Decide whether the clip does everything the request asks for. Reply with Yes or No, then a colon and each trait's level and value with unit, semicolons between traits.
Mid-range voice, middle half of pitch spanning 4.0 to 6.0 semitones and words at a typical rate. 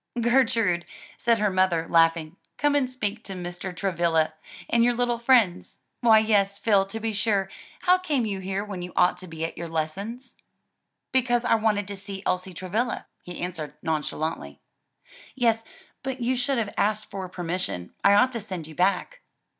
No: high, 200 Hz; average, 4.8 semitones; average, 175 wpm